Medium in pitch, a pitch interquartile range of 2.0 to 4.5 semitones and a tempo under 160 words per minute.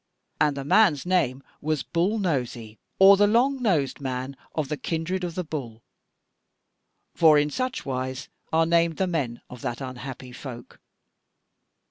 No: medium, 150 Hz; wide, 5.5 semitones; average, 145 wpm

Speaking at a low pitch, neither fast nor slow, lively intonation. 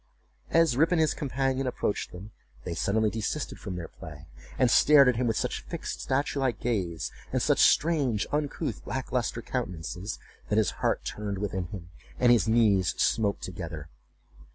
Yes: low, 110 Hz; average, 170 wpm; wide, 6.2 semitones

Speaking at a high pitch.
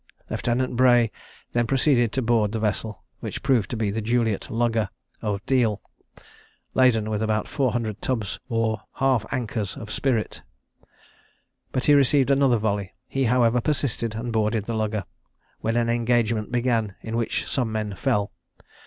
No: low, 115 Hz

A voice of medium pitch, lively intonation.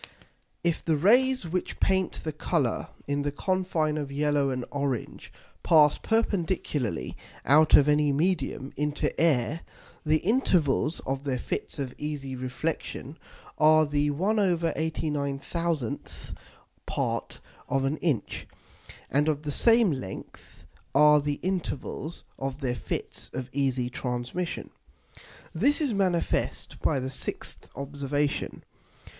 No: medium, 150 Hz; average, 3.6 semitones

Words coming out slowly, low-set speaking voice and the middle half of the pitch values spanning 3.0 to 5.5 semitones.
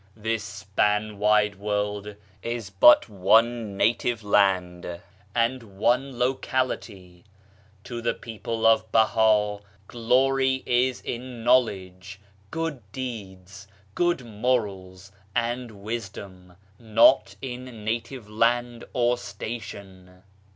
Yes: slow, 100 wpm; low, 110 Hz; average, 3.4 semitones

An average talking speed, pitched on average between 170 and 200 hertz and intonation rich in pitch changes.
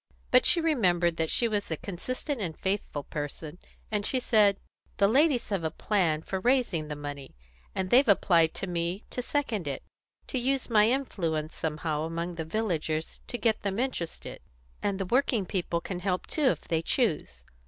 Yes: average, 180 wpm; high, 190 Hz; wide, 6.4 semitones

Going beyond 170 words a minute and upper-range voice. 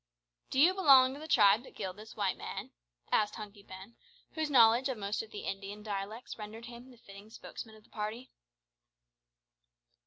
Yes: average, 180 wpm; high, 220 Hz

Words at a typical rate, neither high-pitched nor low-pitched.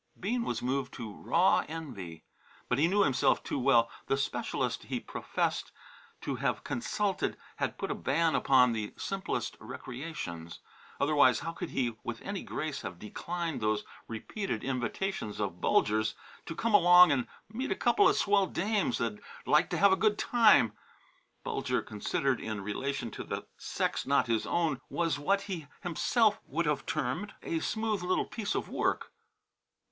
Yes: average, 160 wpm; medium, 150 Hz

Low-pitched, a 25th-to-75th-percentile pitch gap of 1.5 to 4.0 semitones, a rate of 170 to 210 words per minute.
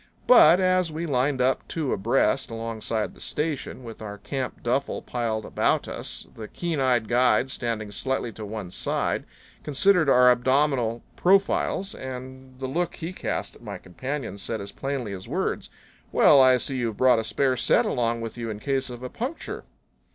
Yes: low, 130 Hz; average, 3.5 semitones; average, 175 wpm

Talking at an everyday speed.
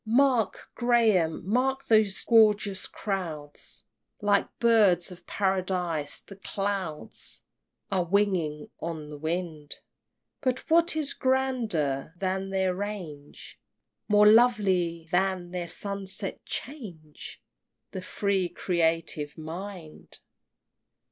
No: slow, 100 wpm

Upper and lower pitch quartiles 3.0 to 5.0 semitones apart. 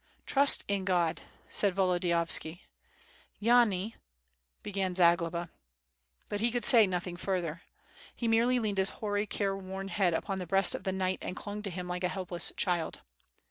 No: narrow, 2.6 semitones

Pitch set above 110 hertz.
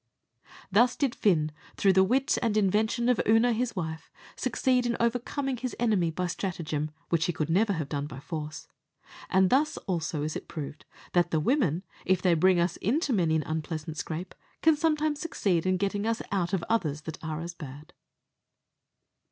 Yes: medium, 185 Hz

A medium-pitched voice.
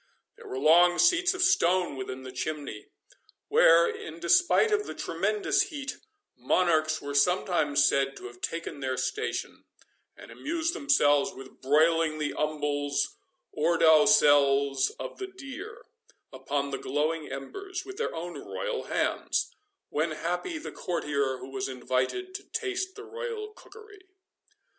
Yes: medium, 165 Hz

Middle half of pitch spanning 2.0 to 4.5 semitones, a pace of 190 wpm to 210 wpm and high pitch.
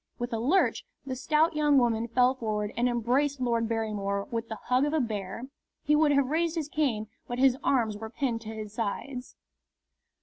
Yes: average, 4.0 semitones; average, 195 wpm; high, 245 Hz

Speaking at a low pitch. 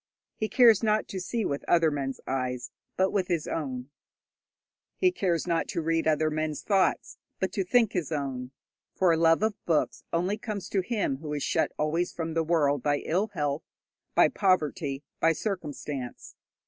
No: medium, 165 Hz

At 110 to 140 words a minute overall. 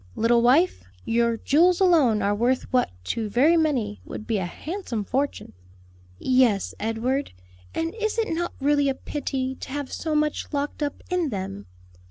No: average, 165 wpm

